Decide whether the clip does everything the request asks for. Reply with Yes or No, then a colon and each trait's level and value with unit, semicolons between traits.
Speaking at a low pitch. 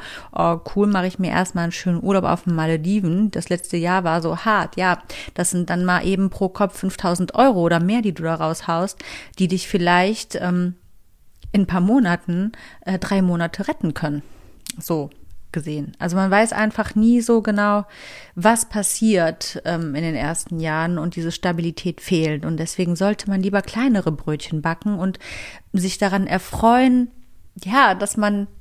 No: medium, 185 Hz